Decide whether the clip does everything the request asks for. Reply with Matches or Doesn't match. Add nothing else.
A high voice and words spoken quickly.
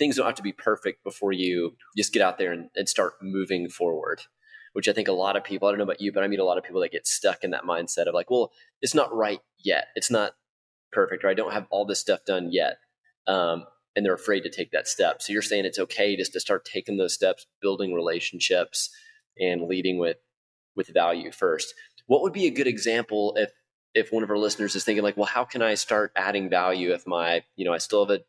Doesn't match